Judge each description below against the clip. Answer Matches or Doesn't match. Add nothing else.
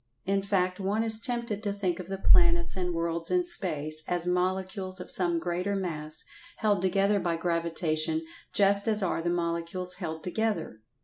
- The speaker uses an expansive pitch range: Doesn't match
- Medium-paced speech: Matches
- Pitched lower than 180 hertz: Doesn't match